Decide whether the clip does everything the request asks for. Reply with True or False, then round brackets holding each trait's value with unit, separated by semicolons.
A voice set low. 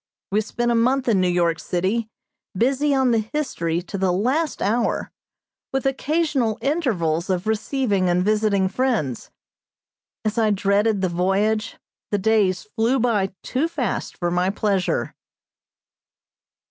False (215 Hz)